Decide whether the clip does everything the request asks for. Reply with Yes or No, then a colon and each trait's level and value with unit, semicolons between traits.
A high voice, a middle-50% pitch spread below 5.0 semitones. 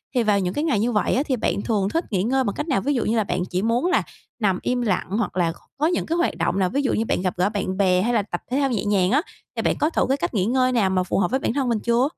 No: high, 225 Hz; average, 5.3 semitones